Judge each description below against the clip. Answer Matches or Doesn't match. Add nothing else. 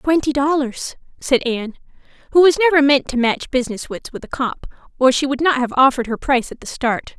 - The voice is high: Matches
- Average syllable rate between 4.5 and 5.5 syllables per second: Doesn't match